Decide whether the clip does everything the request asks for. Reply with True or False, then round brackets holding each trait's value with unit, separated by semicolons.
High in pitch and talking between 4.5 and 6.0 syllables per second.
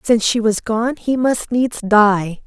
False (225 Hz; 3.9 syllables/s)